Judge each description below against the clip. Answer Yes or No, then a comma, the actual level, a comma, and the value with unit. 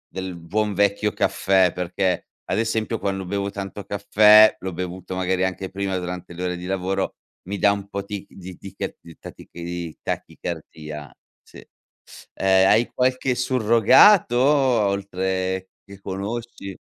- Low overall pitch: Yes, very low, 95 Hz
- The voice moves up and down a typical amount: No, narrow, 2.3 semitones